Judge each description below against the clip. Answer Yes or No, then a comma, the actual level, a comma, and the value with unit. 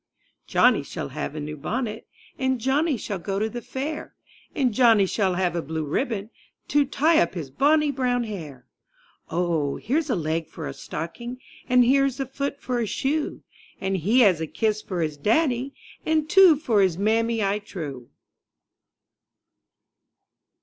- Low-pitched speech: No, high, 220 Hz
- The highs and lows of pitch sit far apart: Yes, wide, 7.4 semitones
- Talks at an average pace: Yes, average, 165 wpm